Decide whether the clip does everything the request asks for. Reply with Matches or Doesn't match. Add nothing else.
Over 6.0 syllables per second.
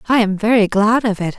Doesn't match